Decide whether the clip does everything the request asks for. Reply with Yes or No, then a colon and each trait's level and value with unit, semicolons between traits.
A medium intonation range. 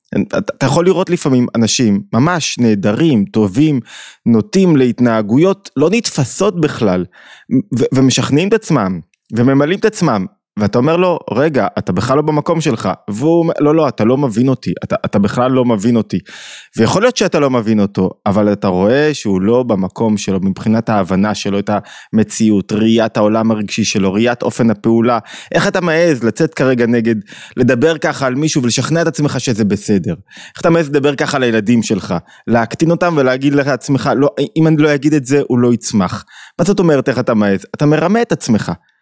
No: wide, 5.7 semitones